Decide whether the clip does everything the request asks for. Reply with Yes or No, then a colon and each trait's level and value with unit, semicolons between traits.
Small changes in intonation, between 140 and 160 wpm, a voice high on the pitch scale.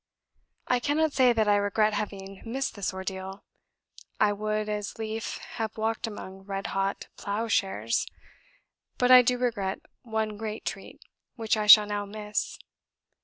Yes: narrow, 2.0 semitones; average, 150 wpm; high, 215 Hz